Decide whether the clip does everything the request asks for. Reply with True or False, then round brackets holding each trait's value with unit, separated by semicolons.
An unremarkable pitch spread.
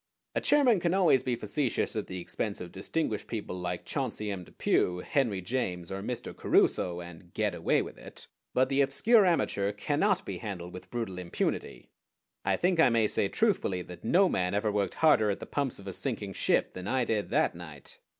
False (7.1 semitones)